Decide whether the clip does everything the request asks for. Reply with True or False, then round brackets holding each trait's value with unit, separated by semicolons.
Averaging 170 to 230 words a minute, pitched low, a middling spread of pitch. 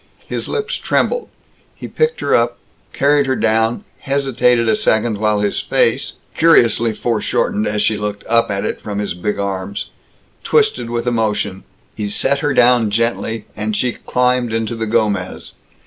False (160 wpm; 115 Hz; 3.0 semitones)